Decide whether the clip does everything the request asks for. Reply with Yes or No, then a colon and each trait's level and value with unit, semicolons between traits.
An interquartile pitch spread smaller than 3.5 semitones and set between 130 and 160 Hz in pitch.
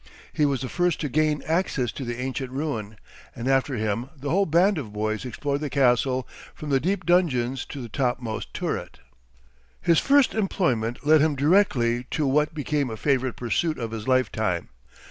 No: average, 4.2 semitones; low, 135 Hz